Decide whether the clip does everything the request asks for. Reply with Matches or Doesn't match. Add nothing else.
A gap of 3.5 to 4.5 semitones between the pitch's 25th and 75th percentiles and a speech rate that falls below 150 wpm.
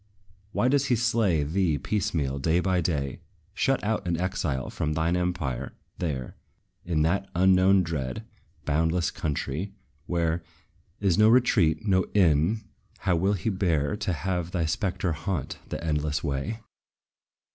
Matches